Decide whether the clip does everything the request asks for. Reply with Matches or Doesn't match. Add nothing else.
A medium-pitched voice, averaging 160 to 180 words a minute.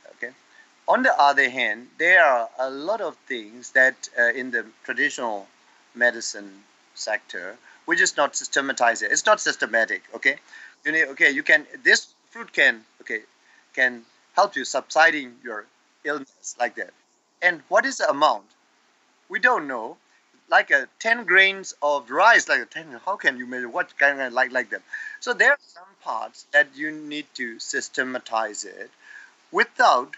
Matches